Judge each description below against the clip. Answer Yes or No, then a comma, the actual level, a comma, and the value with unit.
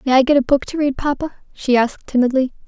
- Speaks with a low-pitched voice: No, very high, 270 Hz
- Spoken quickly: Yes, fast, 245 wpm